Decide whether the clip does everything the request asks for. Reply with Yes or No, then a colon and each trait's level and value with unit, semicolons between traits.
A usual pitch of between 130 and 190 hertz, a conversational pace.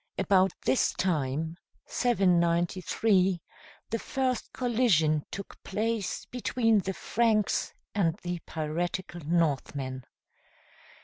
No: medium, 185 Hz; slow, 85 wpm